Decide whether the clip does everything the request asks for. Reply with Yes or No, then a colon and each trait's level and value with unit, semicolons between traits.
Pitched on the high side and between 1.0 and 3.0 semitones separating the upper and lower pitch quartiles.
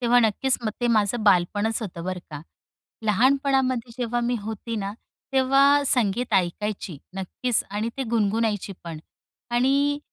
No: high, 230 Hz; average, 3.8 semitones